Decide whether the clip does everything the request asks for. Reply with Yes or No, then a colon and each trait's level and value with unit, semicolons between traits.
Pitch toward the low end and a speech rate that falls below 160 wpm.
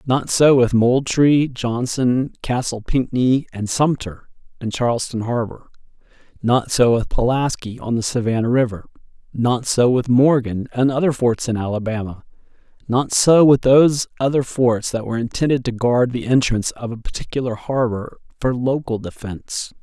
Yes: low, 125 Hz; average, 150 wpm